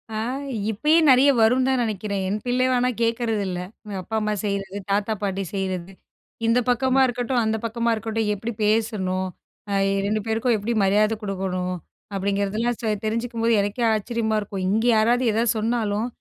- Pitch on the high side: Yes, high, 220 Hz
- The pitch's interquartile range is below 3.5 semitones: Yes, average, 2.8 semitones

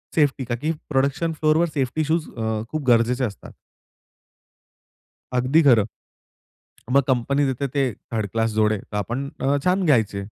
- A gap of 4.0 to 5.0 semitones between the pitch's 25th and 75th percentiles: Yes, average, 4.6 semitones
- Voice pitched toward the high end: No, low, 130 Hz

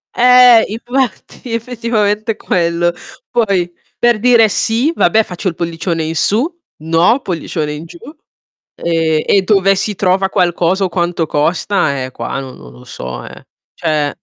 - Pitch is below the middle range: No, medium, 185 Hz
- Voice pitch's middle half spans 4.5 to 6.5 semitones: Yes, average, 5.3 semitones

